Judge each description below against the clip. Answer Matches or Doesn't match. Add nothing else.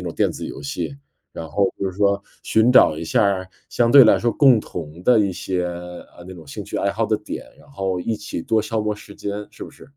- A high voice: Doesn't match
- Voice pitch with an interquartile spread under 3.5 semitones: Doesn't match